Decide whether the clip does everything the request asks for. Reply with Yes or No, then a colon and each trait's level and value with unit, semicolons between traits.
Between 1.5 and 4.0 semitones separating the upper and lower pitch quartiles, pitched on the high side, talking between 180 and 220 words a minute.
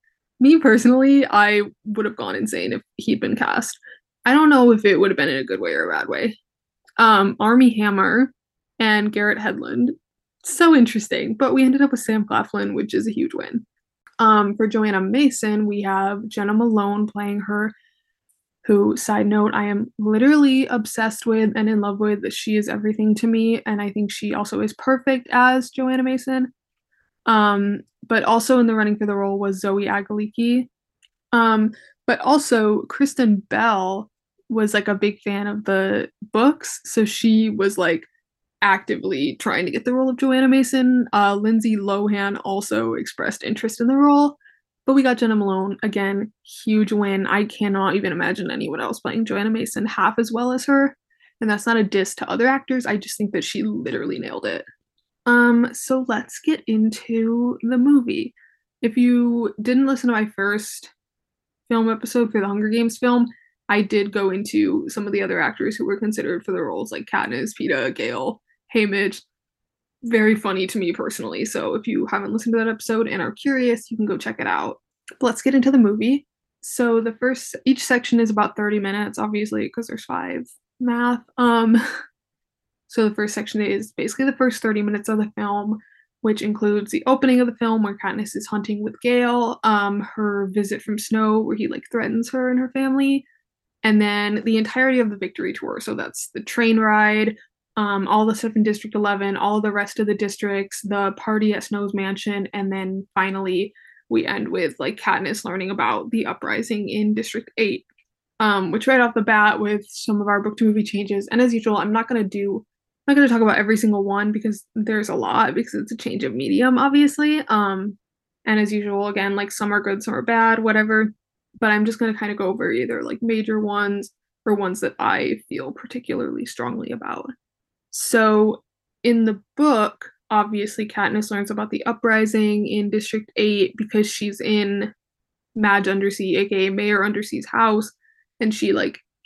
Yes: average, 3.0 semitones; high, 220 Hz; average, 185 wpm